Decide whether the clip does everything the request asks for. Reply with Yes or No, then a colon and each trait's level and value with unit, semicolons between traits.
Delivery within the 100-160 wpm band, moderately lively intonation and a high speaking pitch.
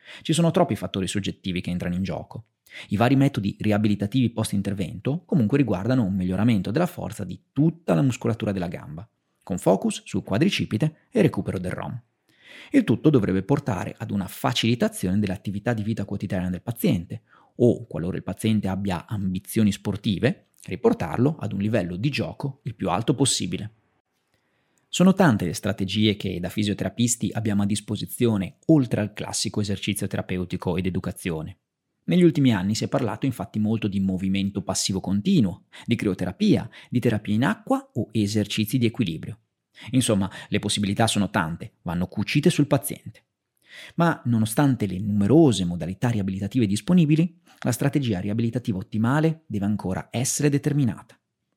No: average, 150 wpm; average, 4.9 semitones; low, 105 Hz